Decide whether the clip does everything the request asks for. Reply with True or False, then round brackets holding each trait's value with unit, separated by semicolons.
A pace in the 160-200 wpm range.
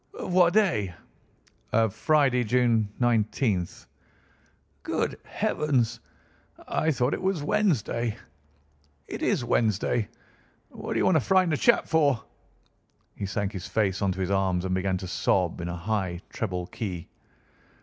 False (140 wpm)